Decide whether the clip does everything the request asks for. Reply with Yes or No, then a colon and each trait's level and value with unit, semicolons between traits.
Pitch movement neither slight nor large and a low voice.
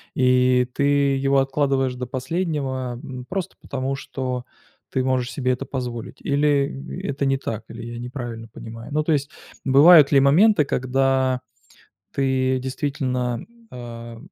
No: narrow, 1.9 semitones; low, 130 Hz